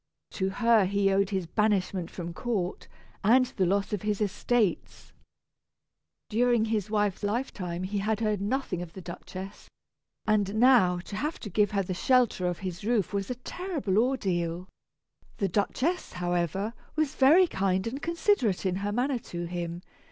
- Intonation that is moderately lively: Yes, average, 4.1 semitones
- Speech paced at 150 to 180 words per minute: Yes, average, 160 wpm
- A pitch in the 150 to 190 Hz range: No, high, 205 Hz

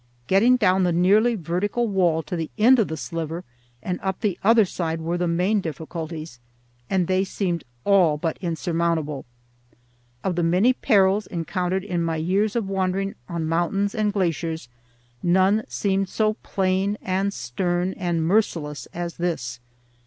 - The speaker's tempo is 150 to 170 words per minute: Yes, average, 155 wpm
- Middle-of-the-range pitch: Yes, medium, 180 Hz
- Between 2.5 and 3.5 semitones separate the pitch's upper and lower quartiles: Yes, average, 2.9 semitones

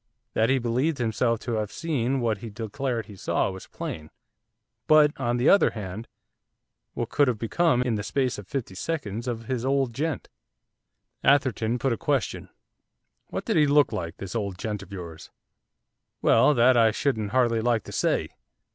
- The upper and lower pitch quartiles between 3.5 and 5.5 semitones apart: Yes, average, 3.8 semitones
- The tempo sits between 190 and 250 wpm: No, average, 175 wpm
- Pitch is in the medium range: No, low, 120 Hz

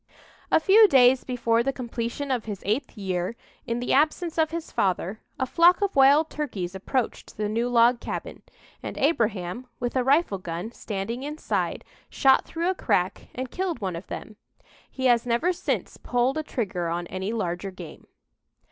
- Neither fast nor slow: Yes, average, 175 wpm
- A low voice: No, high, 240 Hz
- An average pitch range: No, wide, 6.1 semitones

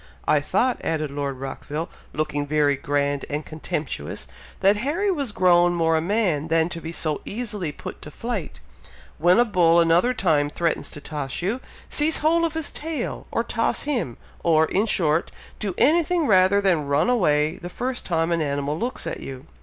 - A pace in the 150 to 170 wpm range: No, average, 180 wpm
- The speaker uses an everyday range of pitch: No, wide, 7.3 semitones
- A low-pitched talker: No, medium, 170 Hz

